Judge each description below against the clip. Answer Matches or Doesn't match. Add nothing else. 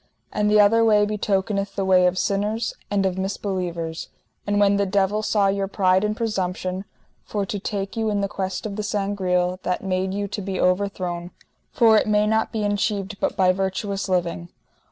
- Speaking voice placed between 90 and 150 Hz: Doesn't match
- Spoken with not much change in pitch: Matches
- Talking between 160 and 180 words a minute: Doesn't match